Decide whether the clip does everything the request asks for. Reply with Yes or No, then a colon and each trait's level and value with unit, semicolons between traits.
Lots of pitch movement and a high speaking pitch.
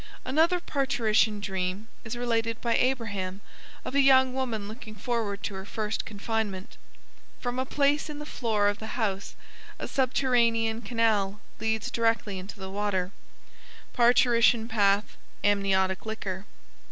No: average, 3.3 semitones; high, 220 Hz